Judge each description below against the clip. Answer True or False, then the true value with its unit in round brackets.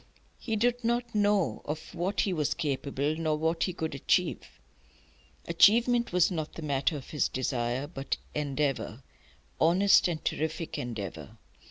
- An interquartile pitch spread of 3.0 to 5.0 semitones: False (5.5 semitones)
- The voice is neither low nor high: True (160 Hz)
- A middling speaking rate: True (145 wpm)